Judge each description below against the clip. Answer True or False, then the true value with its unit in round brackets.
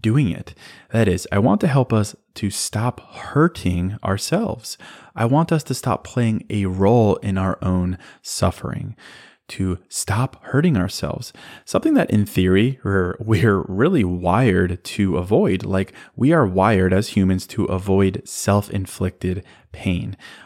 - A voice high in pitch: False (100 Hz)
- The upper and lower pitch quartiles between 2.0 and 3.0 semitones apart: False (3.6 semitones)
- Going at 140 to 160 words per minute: True (145 wpm)